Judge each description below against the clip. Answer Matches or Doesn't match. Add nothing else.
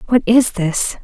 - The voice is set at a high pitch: Matches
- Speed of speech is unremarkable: Matches